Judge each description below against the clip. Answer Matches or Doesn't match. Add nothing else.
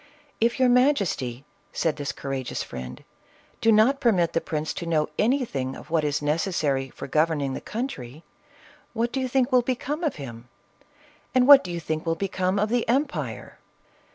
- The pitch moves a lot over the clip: Matches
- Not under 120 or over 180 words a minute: Doesn't match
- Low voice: Doesn't match